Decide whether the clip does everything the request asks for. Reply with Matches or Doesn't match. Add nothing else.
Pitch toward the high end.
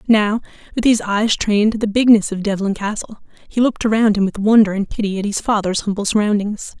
Matches